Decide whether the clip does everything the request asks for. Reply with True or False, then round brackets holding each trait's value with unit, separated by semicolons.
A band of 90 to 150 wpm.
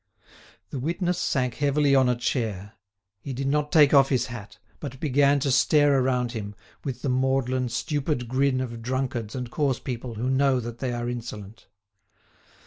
False (170 wpm)